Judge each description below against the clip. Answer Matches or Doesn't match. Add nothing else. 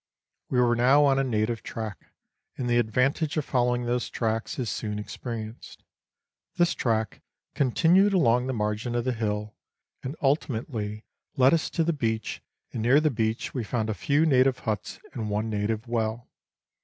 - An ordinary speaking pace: Matches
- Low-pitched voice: Matches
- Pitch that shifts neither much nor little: Matches